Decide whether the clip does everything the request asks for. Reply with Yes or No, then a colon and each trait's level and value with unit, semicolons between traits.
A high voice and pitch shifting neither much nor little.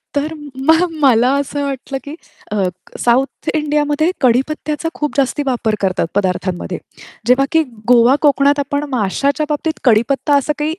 Yes: very high, 275 Hz; average, 3.6 semitones